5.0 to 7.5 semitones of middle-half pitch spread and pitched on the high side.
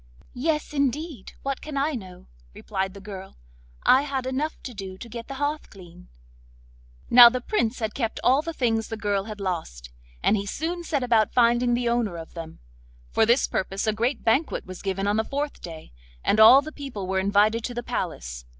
Yes: wide, 5.6 semitones; high, 230 Hz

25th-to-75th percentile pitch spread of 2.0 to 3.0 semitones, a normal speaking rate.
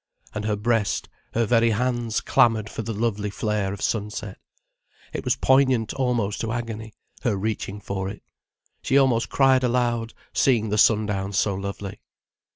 Yes: narrow, 2.5 semitones; average, 155 wpm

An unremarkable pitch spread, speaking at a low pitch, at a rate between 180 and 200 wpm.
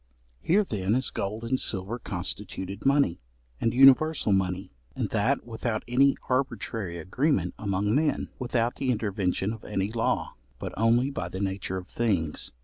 No: average, 4.9 semitones; low, 110 Hz; average, 150 wpm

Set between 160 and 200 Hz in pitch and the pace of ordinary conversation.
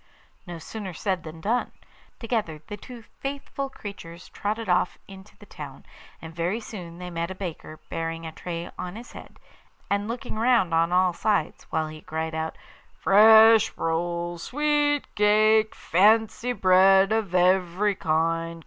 Yes: high, 190 Hz; average, 150 wpm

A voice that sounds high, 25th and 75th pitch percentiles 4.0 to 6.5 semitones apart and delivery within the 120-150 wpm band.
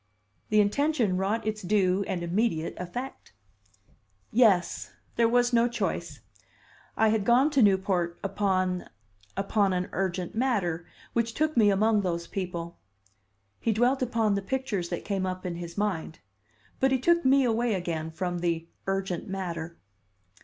Yes: high, 195 Hz; average, 4.6 semitones; average, 145 wpm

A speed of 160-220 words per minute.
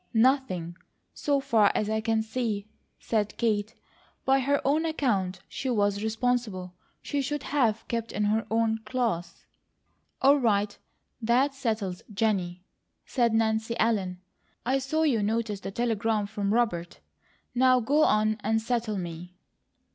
No: average, 140 wpm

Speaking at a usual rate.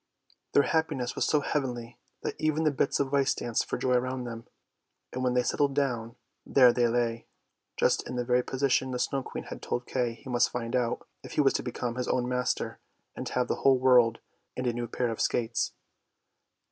No: fast, 210 wpm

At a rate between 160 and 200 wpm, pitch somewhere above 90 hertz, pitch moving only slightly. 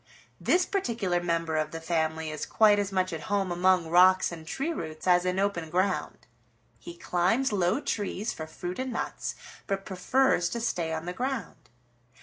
No: average, 175 wpm; medium, 185 Hz; average, 4.0 semitones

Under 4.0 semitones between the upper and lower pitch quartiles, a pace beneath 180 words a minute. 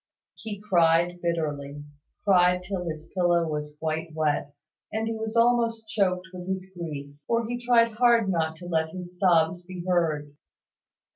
No: average, 4.5 semitones; average, 155 wpm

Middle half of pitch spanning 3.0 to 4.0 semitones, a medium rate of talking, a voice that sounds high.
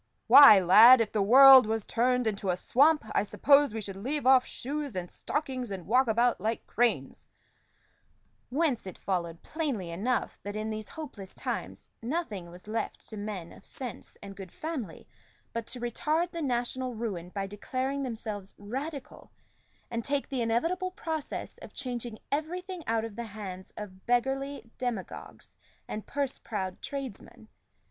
No: average, 5.0 semitones; average, 155 wpm; high, 235 Hz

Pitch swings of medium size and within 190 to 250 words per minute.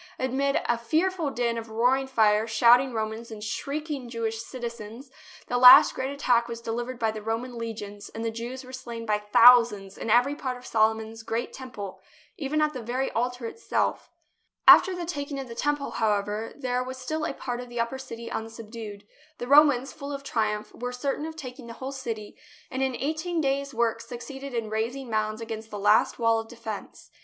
Yes: average, 3.0 semitones; average, 195 wpm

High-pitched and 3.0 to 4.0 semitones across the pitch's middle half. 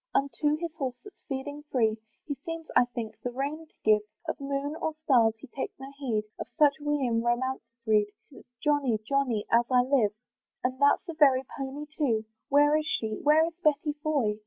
Yes: very high, 275 Hz; average, 3.7 semitones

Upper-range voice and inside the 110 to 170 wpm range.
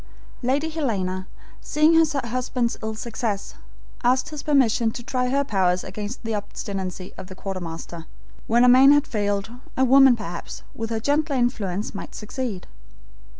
Yes: high, 230 Hz; average, 150 wpm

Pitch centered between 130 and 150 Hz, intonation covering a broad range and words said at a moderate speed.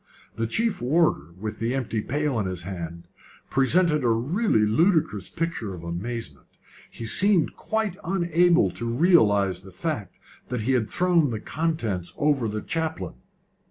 No: low, 120 Hz; wide, 8.0 semitones; average, 150 wpm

